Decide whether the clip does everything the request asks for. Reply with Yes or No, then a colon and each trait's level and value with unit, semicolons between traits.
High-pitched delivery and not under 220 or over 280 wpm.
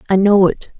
Yes: high, 195 Hz; fast, 225 wpm